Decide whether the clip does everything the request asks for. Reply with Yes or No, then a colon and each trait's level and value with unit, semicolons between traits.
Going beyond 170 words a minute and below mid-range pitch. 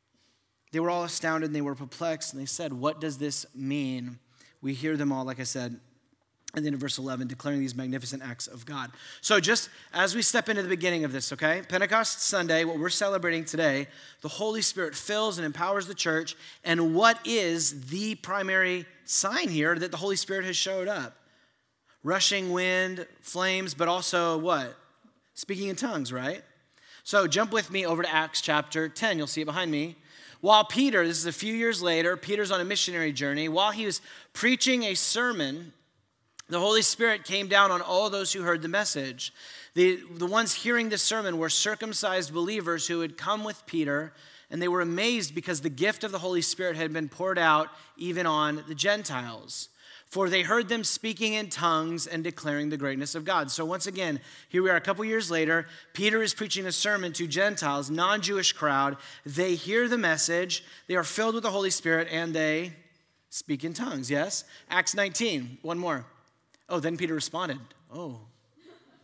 No: average, 190 wpm; medium, 170 Hz